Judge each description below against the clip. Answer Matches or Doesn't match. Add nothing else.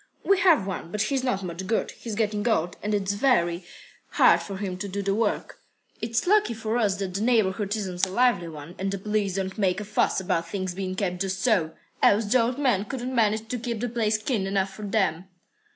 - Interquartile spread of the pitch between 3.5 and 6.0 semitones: Doesn't match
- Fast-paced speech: Matches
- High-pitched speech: Matches